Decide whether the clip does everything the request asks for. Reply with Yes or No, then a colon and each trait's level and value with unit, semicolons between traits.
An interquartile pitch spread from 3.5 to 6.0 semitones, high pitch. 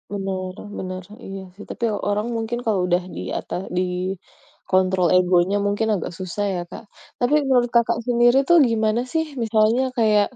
Yes: average, 4.0 semitones; high, 210 Hz